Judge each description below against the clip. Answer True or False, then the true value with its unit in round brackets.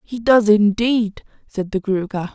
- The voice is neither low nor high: False (210 Hz)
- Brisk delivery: False (155 wpm)